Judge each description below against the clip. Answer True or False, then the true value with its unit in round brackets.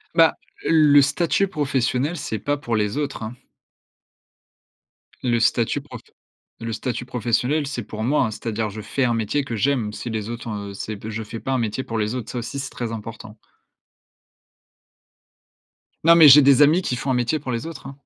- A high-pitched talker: False (125 Hz)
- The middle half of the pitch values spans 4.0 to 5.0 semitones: True (4.3 semitones)